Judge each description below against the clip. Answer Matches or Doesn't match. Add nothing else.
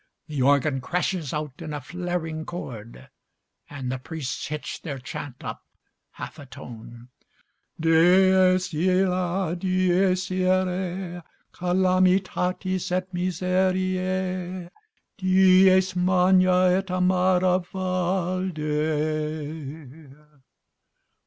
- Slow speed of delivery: Matches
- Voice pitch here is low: Doesn't match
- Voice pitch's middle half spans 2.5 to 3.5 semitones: Matches